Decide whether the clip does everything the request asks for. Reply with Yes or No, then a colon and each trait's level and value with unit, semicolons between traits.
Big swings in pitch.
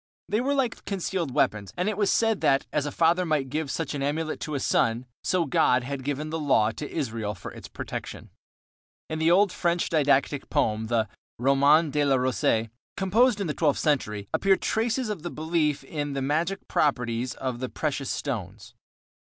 No: average, 4.8 semitones